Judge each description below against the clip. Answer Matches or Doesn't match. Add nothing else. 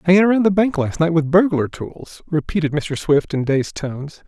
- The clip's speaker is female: Doesn't match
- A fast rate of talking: Matches